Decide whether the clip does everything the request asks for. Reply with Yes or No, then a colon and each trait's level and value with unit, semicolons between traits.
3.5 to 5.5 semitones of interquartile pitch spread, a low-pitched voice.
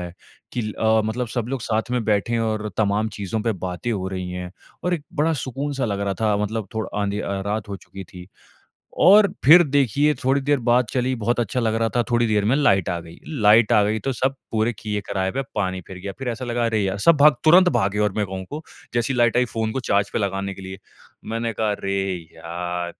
Yes: average, 3.9 semitones; low, 110 Hz